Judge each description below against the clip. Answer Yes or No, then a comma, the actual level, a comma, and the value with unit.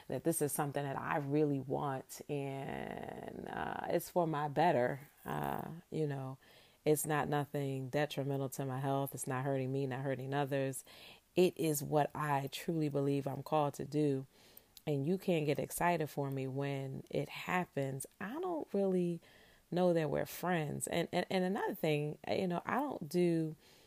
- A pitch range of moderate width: Yes, average, 3.5 semitones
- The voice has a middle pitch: Yes, medium, 145 Hz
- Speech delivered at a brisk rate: No, average, 170 wpm